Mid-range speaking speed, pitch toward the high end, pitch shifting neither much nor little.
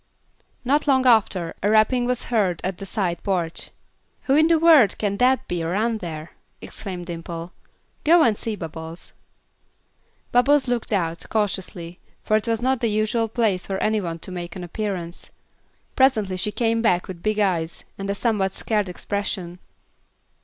Yes: average, 165 wpm; high, 205 Hz; average, 4.6 semitones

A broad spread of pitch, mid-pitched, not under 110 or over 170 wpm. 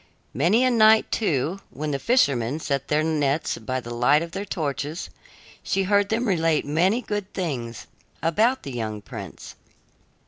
Yes: wide, 6.8 semitones; medium, 160 Hz; average, 160 wpm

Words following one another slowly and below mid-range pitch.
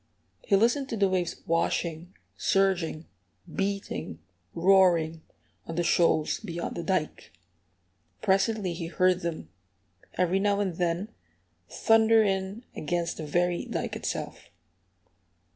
No: slow, 115 wpm; medium, 180 Hz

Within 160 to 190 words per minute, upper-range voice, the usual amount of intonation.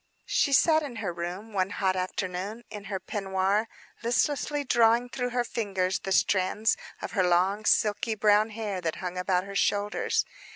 Yes: average, 165 wpm; high, 205 Hz; average, 3.3 semitones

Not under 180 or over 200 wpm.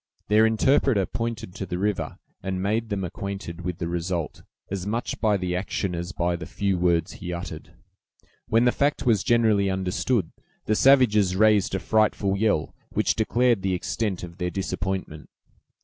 No: average, 165 wpm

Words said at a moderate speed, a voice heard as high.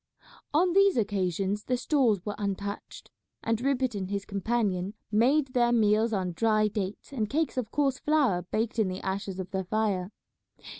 Yes: average, 165 wpm; high, 215 Hz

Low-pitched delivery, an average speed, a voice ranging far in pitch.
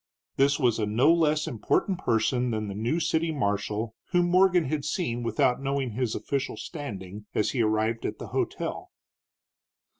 Yes: low, 125 Hz; average, 160 wpm; wide, 5.9 semitones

